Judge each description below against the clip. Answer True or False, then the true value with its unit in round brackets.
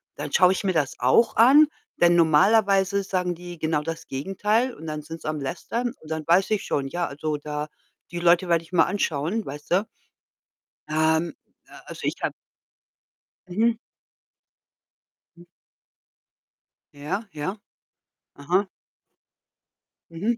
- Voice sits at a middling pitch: True (175 Hz)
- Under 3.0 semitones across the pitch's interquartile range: False (4.2 semitones)